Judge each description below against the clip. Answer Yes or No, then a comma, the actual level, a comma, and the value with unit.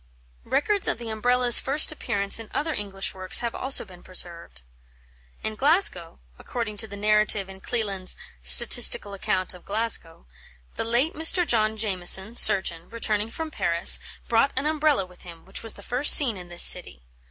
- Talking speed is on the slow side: No, average, 170 wpm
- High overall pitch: Yes, high, 215 Hz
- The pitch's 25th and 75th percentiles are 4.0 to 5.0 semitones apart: Yes, average, 4.7 semitones